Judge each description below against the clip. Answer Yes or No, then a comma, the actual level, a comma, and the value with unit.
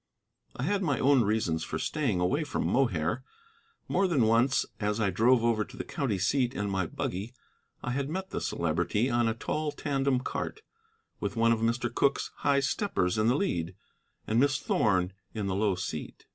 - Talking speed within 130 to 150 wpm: No, average, 185 wpm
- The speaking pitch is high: No, low, 115 Hz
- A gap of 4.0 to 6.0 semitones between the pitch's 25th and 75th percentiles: Yes, wide, 5.5 semitones